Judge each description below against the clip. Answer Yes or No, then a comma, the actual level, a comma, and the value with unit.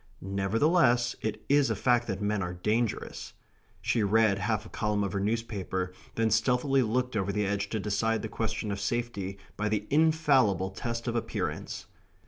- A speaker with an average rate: Yes, average, 170 wpm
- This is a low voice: Yes, low, 110 Hz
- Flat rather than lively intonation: No, average, 3.1 semitones